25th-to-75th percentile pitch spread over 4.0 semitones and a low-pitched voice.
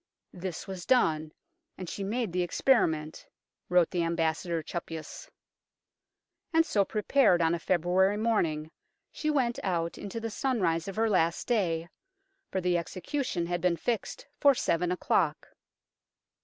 No: average, 4.7 semitones; medium, 180 Hz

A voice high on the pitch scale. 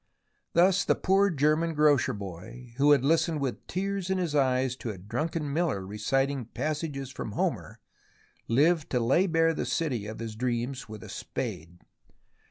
No: medium, 140 Hz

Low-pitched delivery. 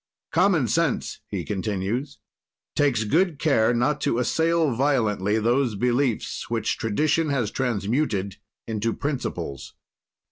Yes: low, 125 Hz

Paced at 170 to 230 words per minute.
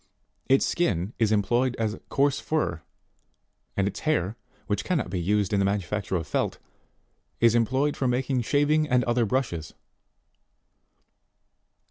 No: average, 140 wpm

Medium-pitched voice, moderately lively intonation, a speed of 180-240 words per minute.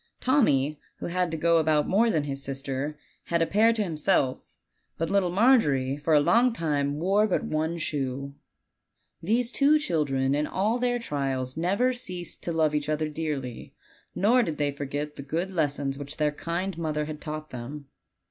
Yes: medium, 155 Hz; average, 4.7 semitones; average, 185 wpm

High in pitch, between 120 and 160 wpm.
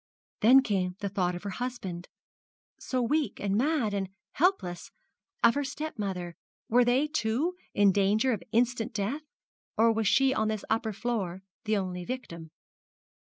Yes: high, 220 Hz; average, 155 wpm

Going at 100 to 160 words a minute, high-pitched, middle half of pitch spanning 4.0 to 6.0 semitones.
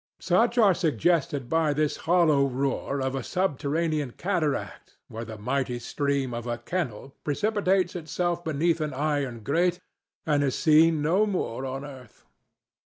No: average, 145 wpm; medium, 150 Hz; average, 4.4 semitones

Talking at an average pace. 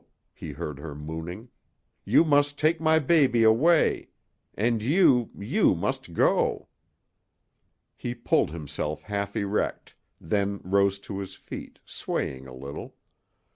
No: slow, 125 wpm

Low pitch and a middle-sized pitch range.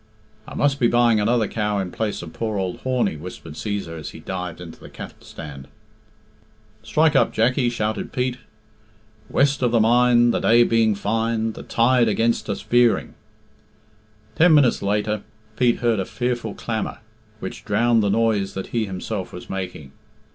Yes: low, 110 Hz; average, 3.3 semitones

